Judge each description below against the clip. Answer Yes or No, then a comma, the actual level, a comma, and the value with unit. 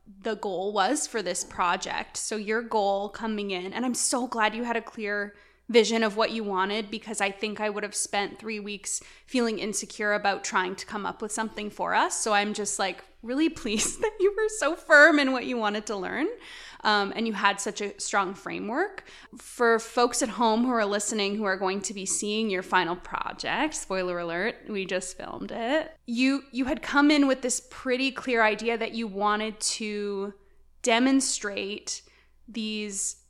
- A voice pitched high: Yes, high, 220 Hz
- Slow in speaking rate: No, average, 195 wpm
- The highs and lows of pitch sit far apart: No, average, 3.3 semitones